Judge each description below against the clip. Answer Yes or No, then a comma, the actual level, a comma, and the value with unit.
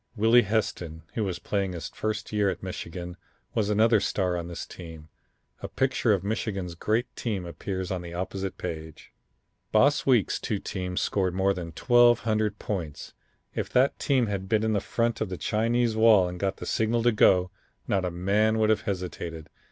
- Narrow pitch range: No, average, 3.6 semitones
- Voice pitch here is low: Yes, low, 100 Hz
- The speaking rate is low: No, average, 180 wpm